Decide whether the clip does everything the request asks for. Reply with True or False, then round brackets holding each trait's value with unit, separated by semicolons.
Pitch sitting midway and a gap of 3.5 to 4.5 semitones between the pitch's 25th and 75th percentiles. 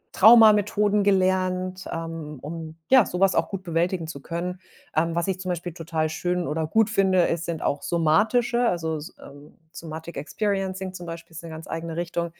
False (170 Hz; 2.7 semitones)